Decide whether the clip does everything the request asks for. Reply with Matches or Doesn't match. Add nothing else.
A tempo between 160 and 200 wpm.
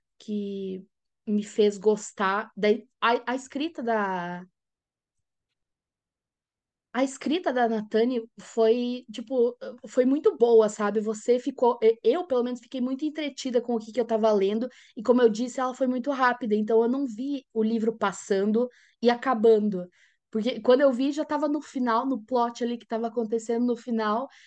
Matches